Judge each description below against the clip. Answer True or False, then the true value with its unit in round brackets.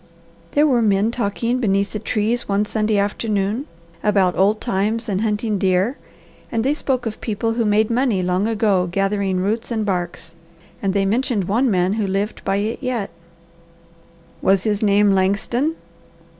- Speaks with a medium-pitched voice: False (210 Hz)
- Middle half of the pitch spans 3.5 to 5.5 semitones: False (2.7 semitones)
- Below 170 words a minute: True (160 wpm)